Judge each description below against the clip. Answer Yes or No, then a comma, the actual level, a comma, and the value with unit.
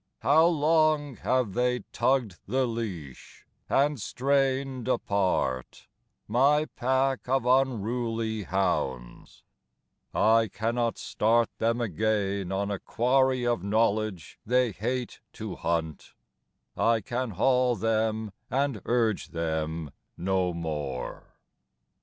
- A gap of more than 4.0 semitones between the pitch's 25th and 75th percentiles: Yes, average, 4.8 semitones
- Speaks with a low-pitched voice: Yes, low, 115 Hz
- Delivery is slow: Yes, slow, 105 wpm